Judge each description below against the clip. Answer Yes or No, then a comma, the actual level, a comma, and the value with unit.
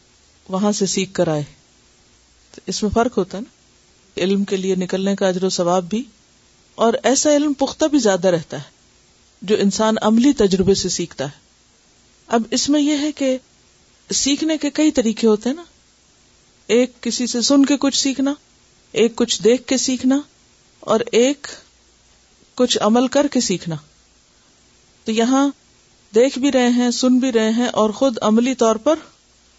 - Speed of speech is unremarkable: Yes, average, 165 wpm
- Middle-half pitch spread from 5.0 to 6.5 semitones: Yes, wide, 5.4 semitones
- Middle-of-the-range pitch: No, high, 230 Hz